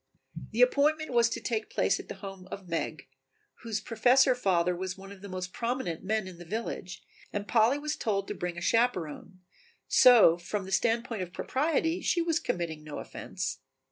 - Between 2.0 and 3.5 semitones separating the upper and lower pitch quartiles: No, average, 5.2 semitones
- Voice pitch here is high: Yes, high, 210 Hz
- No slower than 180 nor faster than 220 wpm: Yes, average, 185 wpm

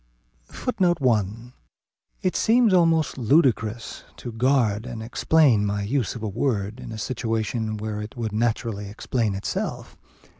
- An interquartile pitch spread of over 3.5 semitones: Yes, average, 3.9 semitones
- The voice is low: Yes, low, 115 Hz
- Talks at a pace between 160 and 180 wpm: No, average, 140 wpm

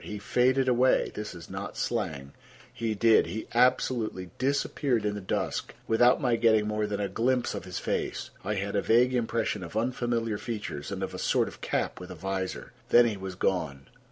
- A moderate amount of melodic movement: Yes, average, 3.9 semitones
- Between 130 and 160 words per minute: No, average, 185 wpm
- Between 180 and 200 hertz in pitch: No, low, 110 Hz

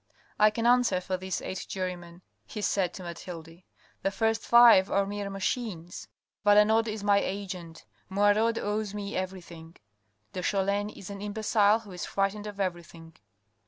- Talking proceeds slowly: No, average, 155 wpm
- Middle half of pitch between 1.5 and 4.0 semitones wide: Yes, narrow, 2.4 semitones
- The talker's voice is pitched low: No, high, 200 Hz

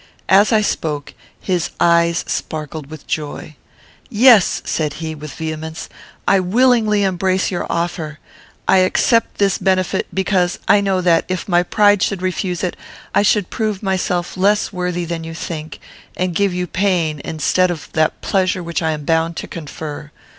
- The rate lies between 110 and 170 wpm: Yes, average, 160 wpm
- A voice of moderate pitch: Yes, medium, 180 Hz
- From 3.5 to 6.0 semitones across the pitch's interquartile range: No, average, 3.1 semitones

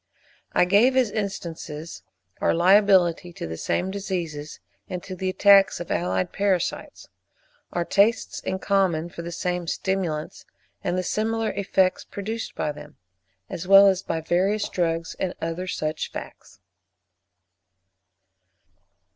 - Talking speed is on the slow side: Yes, slow, 130 wpm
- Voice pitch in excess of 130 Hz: Yes, medium, 185 Hz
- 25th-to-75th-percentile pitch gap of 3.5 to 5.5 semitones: No, average, 3.1 semitones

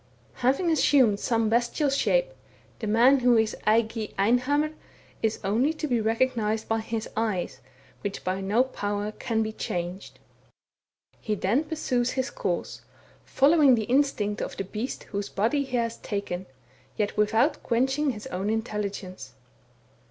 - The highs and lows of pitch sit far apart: No, average, 4.0 semitones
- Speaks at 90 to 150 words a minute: Yes, average, 140 wpm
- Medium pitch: No, high, 225 Hz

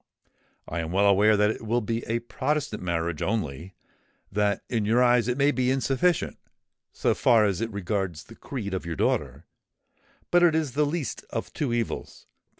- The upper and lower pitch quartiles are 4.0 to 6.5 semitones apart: Yes, average, 4.7 semitones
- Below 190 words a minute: Yes, average, 170 wpm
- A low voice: Yes, low, 115 Hz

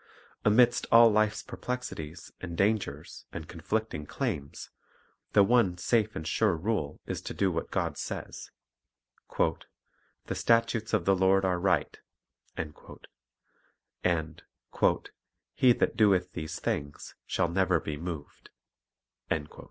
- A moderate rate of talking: No, slow, 125 wpm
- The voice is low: Yes, very low, 95 Hz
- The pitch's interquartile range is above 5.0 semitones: Yes, wide, 5.4 semitones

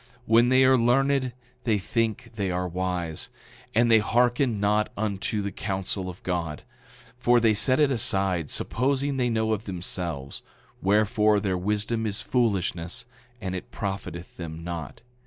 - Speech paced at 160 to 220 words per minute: No, average, 150 wpm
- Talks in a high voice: No, low, 105 Hz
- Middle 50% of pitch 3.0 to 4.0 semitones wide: No, average, 4.4 semitones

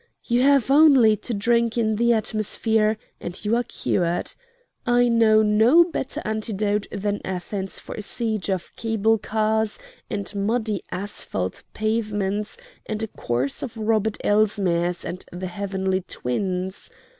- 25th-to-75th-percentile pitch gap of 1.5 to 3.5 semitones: Yes, average, 2.7 semitones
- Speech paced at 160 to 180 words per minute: No, slow, 135 wpm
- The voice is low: No, high, 215 Hz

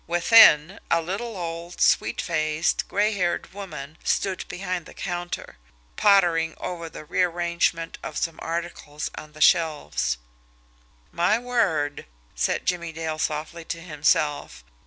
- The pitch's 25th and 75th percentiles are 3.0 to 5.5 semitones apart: No, narrow, 2.6 semitones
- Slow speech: Yes, slow, 125 wpm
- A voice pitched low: No, medium, 170 Hz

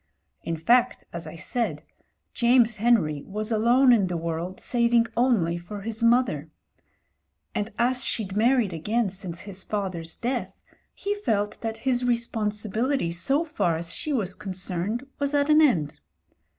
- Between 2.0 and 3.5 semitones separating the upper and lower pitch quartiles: No, average, 5.3 semitones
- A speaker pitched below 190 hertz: No, high, 215 Hz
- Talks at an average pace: Yes, average, 150 wpm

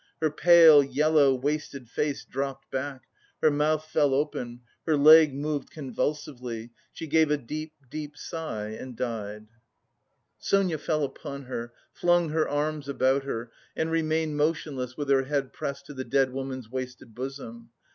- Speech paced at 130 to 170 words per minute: Yes, average, 150 wpm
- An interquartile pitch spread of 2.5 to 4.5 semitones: Yes, average, 2.9 semitones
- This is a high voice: No, medium, 140 Hz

